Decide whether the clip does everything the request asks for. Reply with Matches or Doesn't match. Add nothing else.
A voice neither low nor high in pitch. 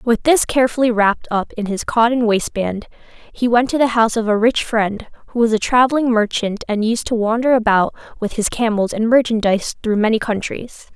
Doesn't match